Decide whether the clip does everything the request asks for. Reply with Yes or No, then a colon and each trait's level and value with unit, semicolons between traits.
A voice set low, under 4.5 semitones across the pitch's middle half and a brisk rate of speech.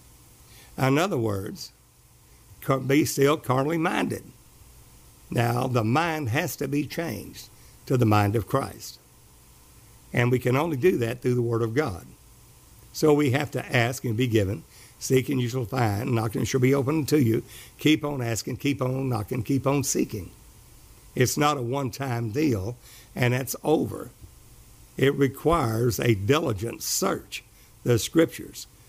No: low, 125 Hz; average, 3.3 semitones; average, 160 wpm